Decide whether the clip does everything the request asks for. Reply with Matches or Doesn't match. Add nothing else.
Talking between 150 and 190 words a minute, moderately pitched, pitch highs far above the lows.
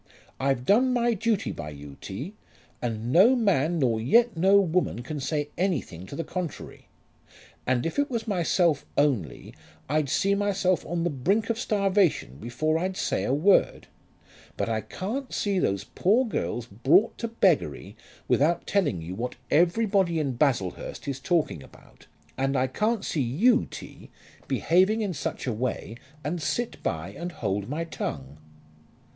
Matches